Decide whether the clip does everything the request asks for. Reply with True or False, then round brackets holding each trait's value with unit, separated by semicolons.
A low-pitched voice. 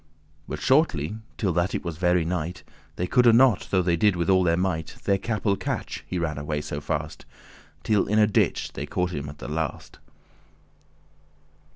True (90 Hz)